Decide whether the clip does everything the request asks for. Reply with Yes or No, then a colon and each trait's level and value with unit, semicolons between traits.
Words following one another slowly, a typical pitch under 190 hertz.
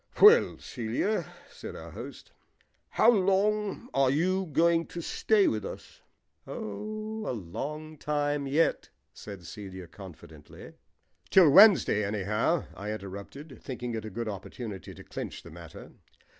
Yes: slow, 130 wpm; low, 135 Hz